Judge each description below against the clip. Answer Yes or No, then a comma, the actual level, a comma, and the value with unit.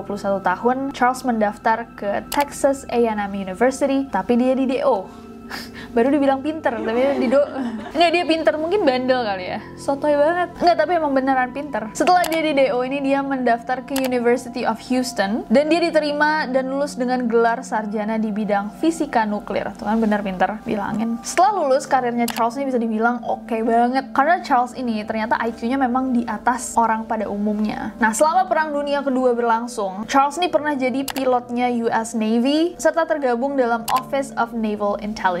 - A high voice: Yes, very high, 250 Hz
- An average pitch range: Yes, average, 3.6 semitones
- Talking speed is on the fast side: Yes, fast, 170 wpm